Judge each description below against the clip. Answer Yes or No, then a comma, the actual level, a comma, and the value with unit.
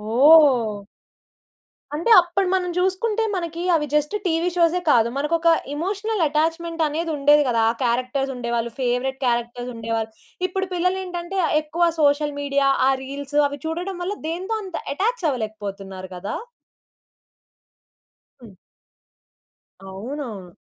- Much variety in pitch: Yes, wide, 6.2 semitones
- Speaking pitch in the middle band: No, very high, 295 Hz